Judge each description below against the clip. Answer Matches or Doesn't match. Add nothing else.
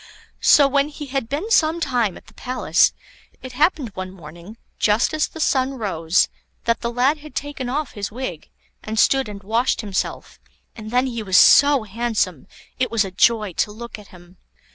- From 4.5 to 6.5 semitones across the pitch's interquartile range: Matches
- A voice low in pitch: Doesn't match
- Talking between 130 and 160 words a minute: Doesn't match